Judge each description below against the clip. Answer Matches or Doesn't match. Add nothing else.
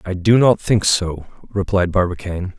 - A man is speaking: Matches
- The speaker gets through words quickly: Doesn't match